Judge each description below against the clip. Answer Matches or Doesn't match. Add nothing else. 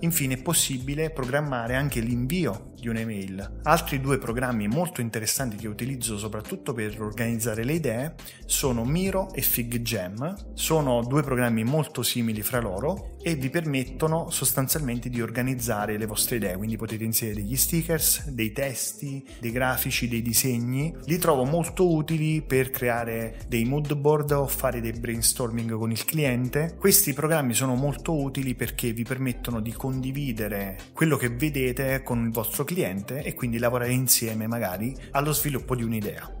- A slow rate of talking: Doesn't match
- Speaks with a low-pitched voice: Matches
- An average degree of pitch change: Matches